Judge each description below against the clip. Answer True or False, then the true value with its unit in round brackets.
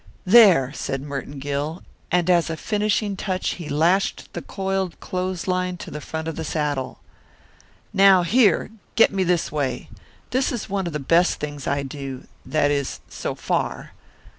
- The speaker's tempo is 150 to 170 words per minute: True (165 wpm)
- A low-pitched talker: False (170 Hz)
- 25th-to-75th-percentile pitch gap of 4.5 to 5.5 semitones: True (4.8 semitones)